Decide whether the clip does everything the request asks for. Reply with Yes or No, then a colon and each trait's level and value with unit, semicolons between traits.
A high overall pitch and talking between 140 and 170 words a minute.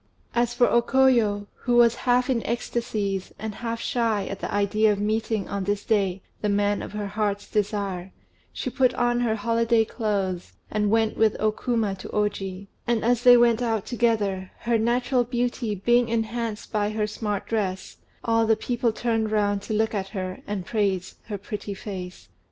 No: high, 215 Hz; average, 180 wpm